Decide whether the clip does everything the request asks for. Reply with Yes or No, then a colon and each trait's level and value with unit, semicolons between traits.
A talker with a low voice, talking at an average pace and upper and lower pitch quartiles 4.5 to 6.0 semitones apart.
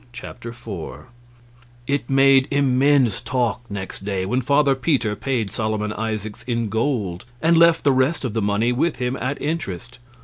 No: low, 125 Hz; average, 160 wpm; average, 4.1 semitones